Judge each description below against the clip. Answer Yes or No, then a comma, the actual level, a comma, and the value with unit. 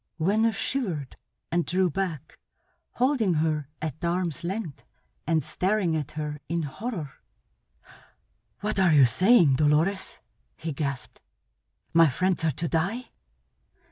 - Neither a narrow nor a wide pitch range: Yes, average, 4.2 semitones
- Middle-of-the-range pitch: Yes, medium, 170 Hz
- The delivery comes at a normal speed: No, slow, 120 wpm